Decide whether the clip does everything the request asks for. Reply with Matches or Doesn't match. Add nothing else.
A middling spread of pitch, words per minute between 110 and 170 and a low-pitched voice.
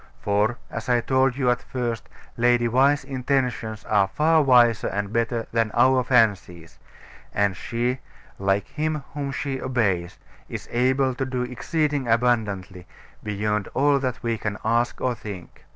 Matches